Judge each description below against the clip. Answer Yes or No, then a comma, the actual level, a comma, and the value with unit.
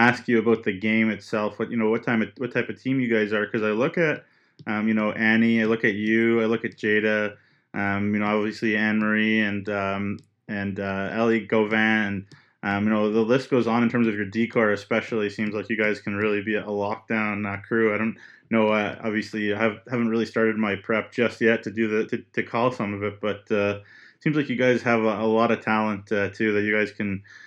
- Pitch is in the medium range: No, low, 110 Hz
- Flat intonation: Yes, narrow, 1.5 semitones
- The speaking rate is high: Yes, fast, 245 wpm